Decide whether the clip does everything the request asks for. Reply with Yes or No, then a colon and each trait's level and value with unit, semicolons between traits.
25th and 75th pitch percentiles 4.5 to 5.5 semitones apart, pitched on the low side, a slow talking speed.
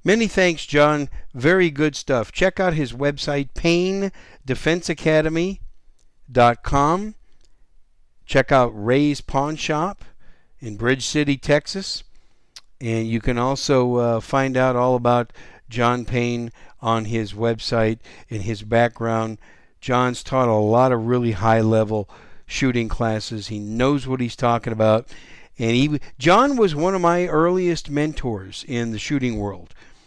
Yes: average, 4.8 semitones; low, 125 Hz; slow, 130 wpm